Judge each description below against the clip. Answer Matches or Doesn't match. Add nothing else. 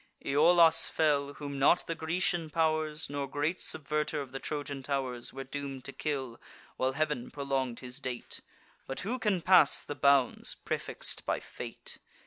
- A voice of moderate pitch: Matches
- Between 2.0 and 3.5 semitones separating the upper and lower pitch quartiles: Matches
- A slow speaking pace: Doesn't match